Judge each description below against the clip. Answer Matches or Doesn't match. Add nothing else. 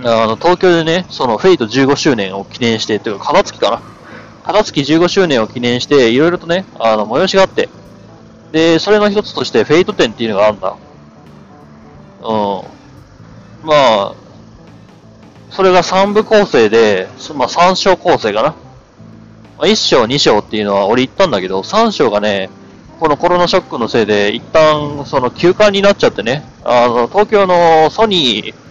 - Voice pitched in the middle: Matches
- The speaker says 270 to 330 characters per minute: Matches